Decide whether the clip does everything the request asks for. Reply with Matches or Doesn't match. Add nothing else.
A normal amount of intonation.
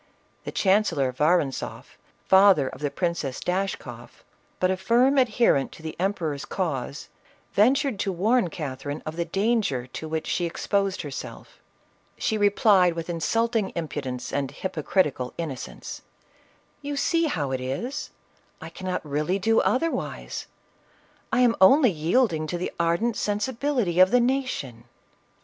Doesn't match